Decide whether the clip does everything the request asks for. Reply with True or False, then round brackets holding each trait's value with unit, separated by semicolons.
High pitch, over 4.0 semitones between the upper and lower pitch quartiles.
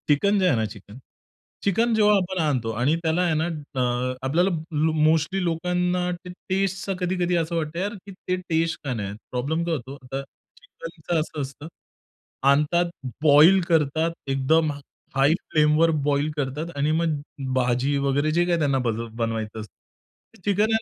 False (160 Hz; 4.5 semitones)